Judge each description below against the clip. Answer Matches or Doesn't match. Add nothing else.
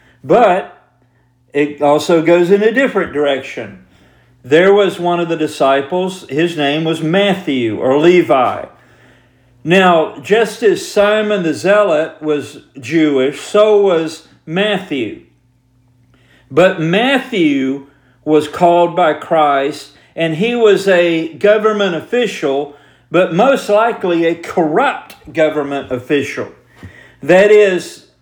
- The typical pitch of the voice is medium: Matches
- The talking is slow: Matches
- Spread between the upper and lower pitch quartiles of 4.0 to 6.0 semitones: Matches